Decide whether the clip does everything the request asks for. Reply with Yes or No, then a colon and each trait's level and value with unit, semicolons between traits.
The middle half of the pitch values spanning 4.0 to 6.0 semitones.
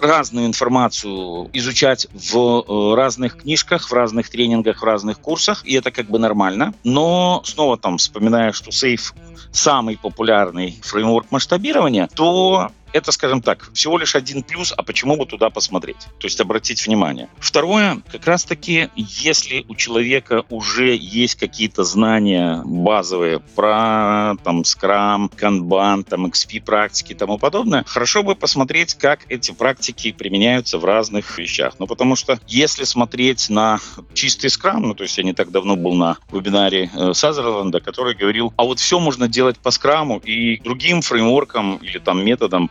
Yes: average, 4.4 semitones